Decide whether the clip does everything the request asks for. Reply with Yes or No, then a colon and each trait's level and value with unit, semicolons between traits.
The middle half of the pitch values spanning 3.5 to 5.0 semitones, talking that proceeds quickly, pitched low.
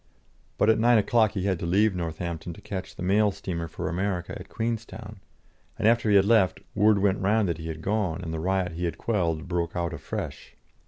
Yes: average, 3.9 semitones; fast, 215 wpm; very low, 95 Hz